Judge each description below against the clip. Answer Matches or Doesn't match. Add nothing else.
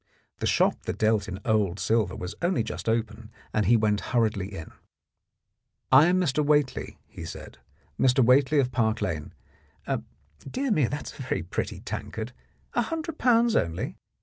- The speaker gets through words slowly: Doesn't match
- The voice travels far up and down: Matches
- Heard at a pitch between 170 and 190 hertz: Doesn't match